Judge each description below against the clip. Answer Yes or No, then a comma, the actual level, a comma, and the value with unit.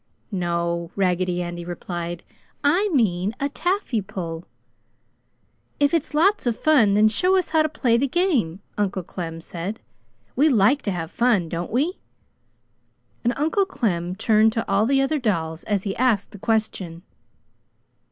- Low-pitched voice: No, high, 210 Hz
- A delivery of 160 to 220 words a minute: No, average, 150 wpm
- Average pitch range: No, wide, 8.0 semitones